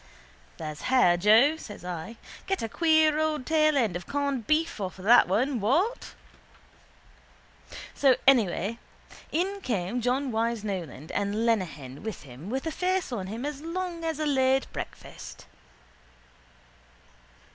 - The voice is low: No, high, 245 Hz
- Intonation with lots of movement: Yes, wide, 7.5 semitones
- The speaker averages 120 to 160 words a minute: Yes, slow, 135 wpm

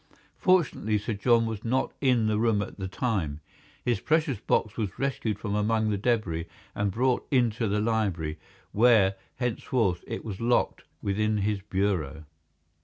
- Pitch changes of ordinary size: Yes, average, 3.2 semitones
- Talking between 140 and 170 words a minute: Yes, average, 155 wpm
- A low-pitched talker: Yes, low, 110 Hz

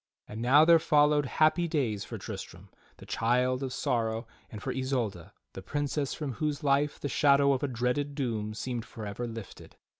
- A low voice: Yes, low, 130 Hz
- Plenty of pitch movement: No, average, 4.2 semitones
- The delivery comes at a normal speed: Yes, average, 175 wpm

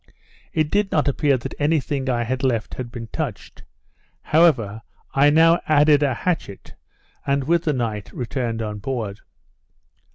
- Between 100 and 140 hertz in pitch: Yes, low, 135 Hz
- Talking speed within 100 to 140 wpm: No, average, 155 wpm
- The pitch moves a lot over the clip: No, average, 4.6 semitones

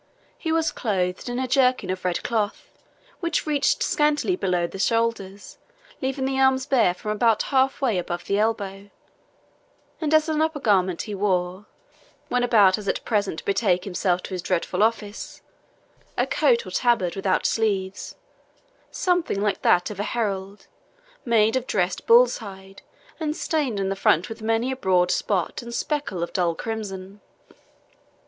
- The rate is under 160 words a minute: No, average, 165 wpm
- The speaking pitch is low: No, high, 210 Hz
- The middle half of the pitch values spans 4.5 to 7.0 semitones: Yes, average, 5.1 semitones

